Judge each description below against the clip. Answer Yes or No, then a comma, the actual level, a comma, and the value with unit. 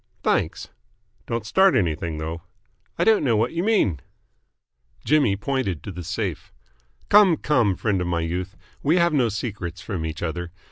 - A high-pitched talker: No, low, 100 Hz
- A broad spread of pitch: Yes, wide, 8.4 semitones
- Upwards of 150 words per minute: Yes, average, 160 wpm